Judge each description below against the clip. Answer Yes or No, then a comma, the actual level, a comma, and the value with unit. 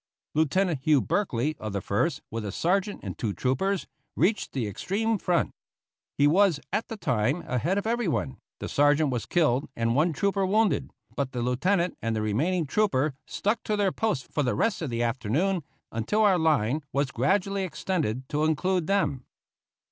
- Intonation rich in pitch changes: Yes, wide, 7.2 semitones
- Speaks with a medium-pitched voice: Yes, medium, 155 Hz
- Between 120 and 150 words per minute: No, average, 175 wpm